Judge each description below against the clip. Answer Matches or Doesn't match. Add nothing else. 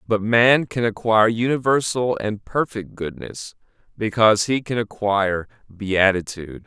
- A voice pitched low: Matches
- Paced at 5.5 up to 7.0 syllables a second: Doesn't match